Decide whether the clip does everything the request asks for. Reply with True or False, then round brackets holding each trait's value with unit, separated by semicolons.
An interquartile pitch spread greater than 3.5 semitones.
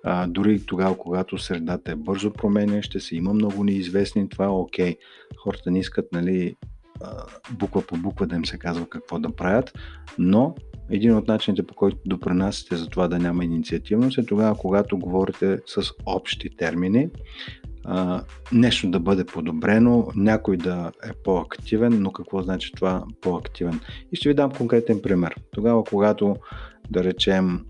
False (2.8 semitones)